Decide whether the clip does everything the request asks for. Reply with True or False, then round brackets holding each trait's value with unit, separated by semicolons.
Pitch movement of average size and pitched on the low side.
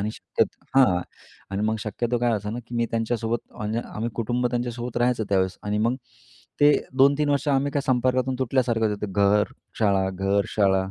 True (3.3 semitones; 115 Hz)